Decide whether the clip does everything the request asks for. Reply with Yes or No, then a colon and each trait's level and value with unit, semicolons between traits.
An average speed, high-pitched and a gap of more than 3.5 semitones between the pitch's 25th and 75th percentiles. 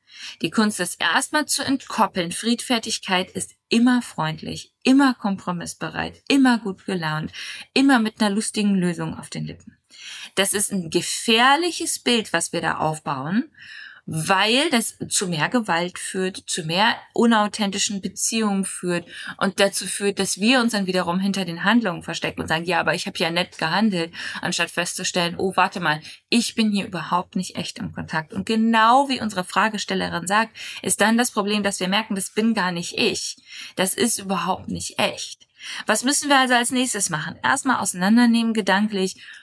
Yes: average, 165 wpm; high, 200 Hz; average, 4.1 semitones